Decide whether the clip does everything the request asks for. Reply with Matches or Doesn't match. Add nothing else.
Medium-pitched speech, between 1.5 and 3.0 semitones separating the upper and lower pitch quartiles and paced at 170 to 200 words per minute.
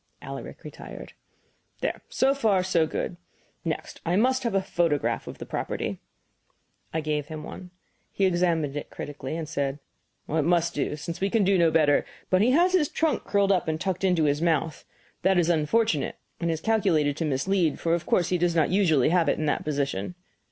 Doesn't match